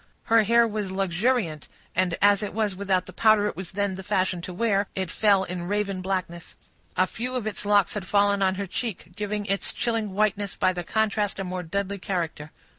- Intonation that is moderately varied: No, narrow, 2.1 semitones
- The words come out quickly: Yes, fast, 210 wpm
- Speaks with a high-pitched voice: Yes, high, 200 Hz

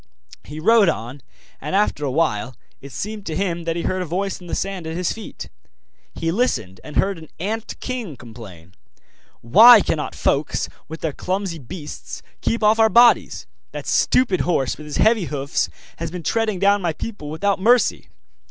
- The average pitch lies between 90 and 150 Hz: No, medium, 175 Hz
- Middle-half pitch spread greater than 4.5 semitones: Yes, wide, 5.6 semitones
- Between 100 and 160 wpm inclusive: No, average, 180 wpm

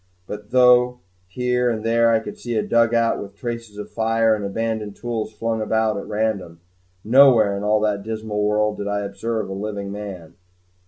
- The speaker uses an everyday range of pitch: No, narrow, 2.0 semitones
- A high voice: No, low, 110 Hz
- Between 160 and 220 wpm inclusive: Yes, average, 180 wpm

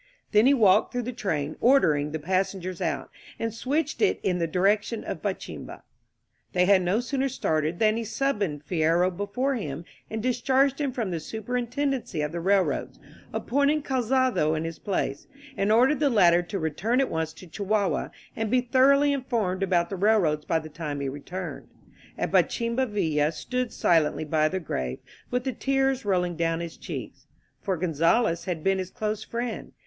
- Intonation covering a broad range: Yes, wide, 6.8 semitones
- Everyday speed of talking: Yes, average, 180 wpm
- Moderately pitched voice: No, high, 200 Hz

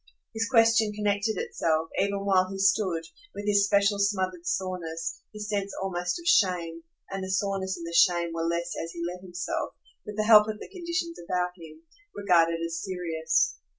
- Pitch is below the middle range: No, high, 190 Hz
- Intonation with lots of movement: No, average, 3.2 semitones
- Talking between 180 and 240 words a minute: Yes, average, 185 wpm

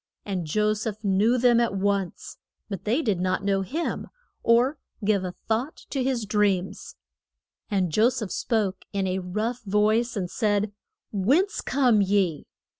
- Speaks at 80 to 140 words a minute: No, average, 155 wpm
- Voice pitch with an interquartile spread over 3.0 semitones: Yes, average, 3.4 semitones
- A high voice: Yes, high, 210 Hz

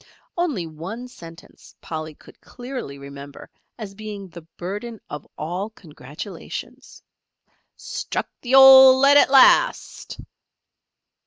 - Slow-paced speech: Yes, slow, 105 wpm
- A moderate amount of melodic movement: No, wide, 8.0 semitones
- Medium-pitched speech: No, high, 200 Hz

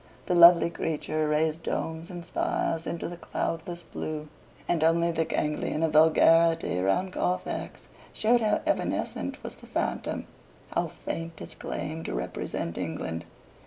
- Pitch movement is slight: Yes, narrow, 1.7 semitones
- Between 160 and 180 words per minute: No, average, 140 wpm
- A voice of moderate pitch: Yes, medium, 165 Hz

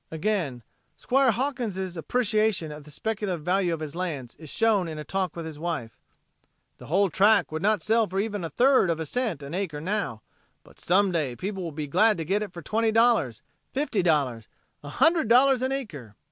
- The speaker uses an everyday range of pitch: No, wide, 5.9 semitones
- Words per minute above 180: Yes, fast, 205 wpm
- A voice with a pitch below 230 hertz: Yes, medium, 185 Hz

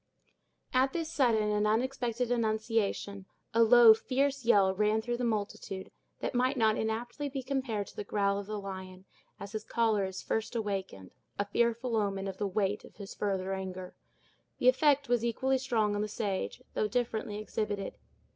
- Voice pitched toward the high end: Yes, high, 220 Hz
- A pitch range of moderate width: Yes, average, 3.3 semitones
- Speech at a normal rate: Yes, average, 170 wpm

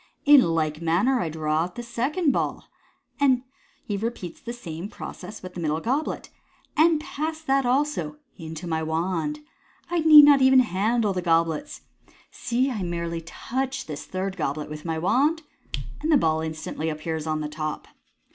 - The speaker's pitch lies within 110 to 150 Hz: No, high, 190 Hz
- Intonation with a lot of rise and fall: Yes, wide, 8.8 semitones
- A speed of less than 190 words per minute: Yes, average, 165 wpm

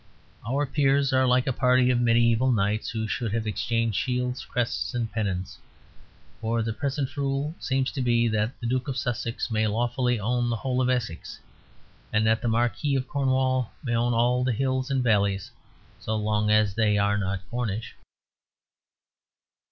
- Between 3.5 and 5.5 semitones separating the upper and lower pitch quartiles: No, average, 2.8 semitones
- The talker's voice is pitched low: Yes, low, 120 Hz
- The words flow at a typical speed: Yes, average, 170 wpm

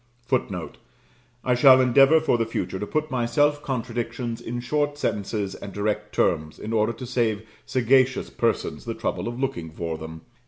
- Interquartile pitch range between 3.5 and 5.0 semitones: Yes, average, 4.1 semitones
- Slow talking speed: No, average, 170 wpm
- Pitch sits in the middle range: No, low, 120 Hz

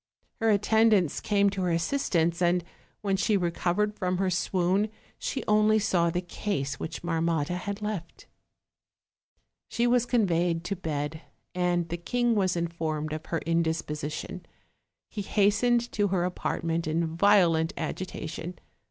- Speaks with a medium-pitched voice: Yes, medium, 180 Hz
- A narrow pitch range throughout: No, average, 3.7 semitones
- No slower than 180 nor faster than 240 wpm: No, slow, 135 wpm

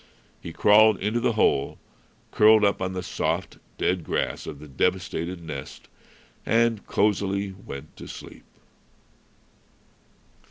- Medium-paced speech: No, slow, 120 wpm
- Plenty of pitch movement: No, average, 4.2 semitones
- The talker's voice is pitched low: Yes, very low, 95 Hz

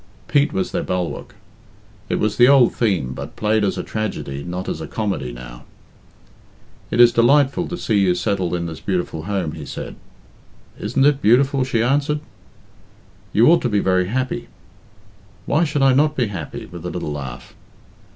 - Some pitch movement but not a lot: No, wide, 7.3 semitones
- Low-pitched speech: Yes, low, 105 Hz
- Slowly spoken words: No, average, 175 wpm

